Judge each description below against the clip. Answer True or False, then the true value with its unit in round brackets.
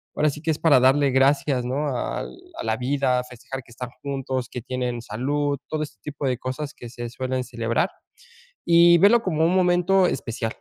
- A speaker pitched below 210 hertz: True (135 Hz)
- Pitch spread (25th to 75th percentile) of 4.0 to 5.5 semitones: False (3.4 semitones)